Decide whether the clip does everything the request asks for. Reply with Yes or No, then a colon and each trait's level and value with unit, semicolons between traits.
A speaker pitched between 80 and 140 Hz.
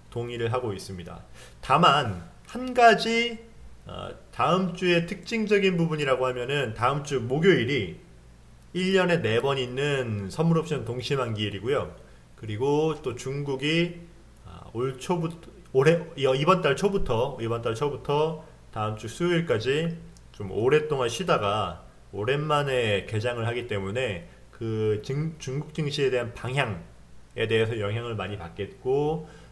Yes: low, 135 Hz